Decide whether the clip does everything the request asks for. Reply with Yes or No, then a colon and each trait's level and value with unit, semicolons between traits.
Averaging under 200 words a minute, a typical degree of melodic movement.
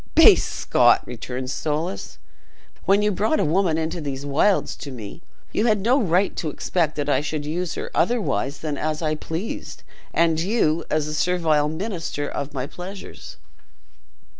Yes: average, 165 wpm; average, 4.2 semitones